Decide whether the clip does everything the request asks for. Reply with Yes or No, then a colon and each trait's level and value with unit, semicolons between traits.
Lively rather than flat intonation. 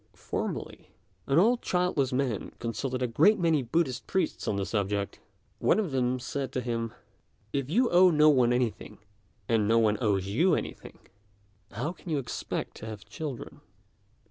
Yes: wide, 5.7 semitones